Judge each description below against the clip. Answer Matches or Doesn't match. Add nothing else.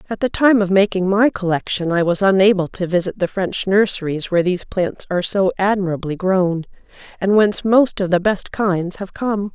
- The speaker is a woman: Matches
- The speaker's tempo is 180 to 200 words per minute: Matches